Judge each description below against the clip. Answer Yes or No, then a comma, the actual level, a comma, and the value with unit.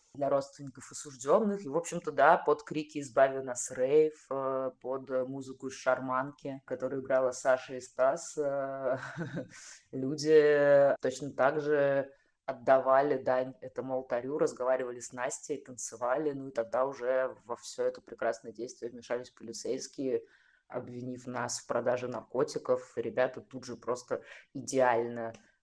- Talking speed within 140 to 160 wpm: No, average, 125 wpm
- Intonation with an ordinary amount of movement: No, narrow, 2.2 semitones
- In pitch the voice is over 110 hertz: Yes, low, 135 Hz